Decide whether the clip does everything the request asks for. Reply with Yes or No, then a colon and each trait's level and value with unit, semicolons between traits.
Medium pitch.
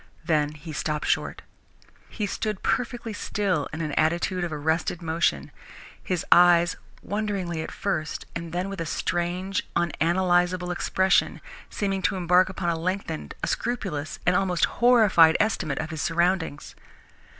Yes: medium, 175 Hz